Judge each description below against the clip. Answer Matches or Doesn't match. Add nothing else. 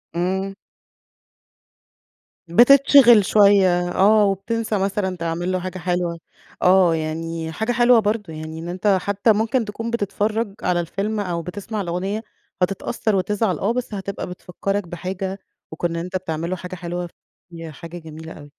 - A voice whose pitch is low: Doesn't match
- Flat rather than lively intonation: Doesn't match